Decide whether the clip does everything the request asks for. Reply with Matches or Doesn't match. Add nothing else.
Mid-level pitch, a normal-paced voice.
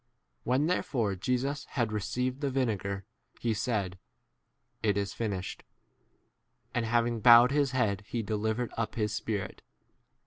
Doesn't match